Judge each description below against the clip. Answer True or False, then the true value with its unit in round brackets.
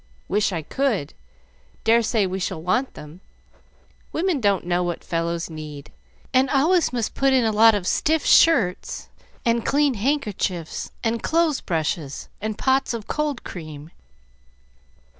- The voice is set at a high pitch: True (215 Hz)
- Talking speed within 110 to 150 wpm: True (140 wpm)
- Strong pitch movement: True (7.5 semitones)